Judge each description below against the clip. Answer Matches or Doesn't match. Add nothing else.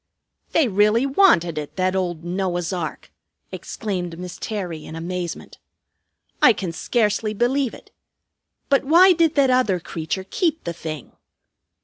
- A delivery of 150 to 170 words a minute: Doesn't match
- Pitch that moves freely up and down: Matches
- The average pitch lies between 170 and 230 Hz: Matches